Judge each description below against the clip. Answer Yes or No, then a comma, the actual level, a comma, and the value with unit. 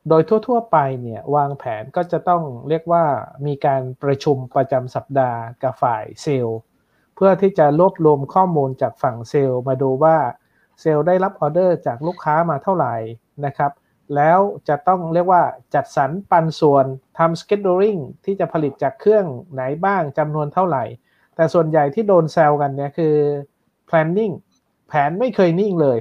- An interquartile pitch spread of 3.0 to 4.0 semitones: No, average, 4.5 semitones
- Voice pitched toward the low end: No, medium, 155 Hz